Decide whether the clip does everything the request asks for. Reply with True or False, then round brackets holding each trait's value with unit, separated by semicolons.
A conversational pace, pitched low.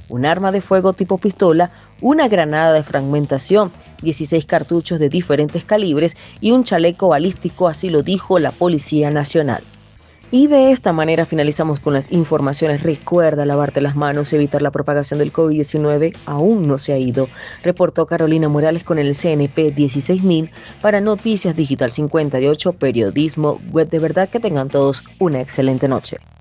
False (155 wpm; 160 Hz)